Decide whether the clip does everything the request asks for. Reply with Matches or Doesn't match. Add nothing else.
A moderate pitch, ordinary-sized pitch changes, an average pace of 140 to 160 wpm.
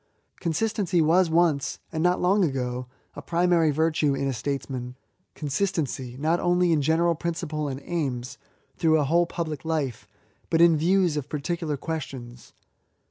Matches